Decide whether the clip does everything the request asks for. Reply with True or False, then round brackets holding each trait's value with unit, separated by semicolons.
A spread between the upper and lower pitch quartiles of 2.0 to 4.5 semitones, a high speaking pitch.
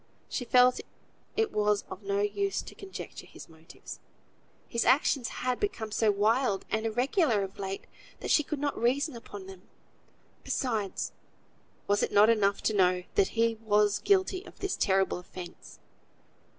False (4.9 semitones; 220 Hz)